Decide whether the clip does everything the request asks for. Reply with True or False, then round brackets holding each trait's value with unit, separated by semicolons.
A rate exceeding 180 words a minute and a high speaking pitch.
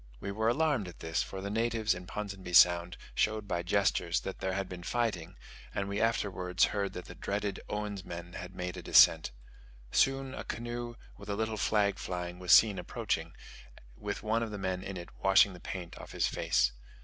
False (195 wpm; 100 Hz)